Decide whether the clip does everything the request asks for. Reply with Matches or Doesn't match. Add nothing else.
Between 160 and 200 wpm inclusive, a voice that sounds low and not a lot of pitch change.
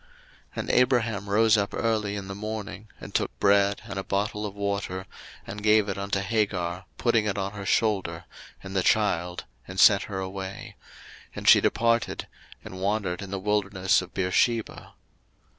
Matches